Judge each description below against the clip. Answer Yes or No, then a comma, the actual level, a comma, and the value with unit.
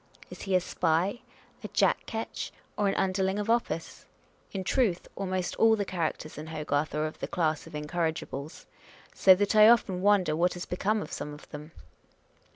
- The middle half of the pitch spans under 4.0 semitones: No, average, 4.3 semitones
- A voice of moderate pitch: Yes, medium, 180 Hz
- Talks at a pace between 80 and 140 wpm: No, average, 180 wpm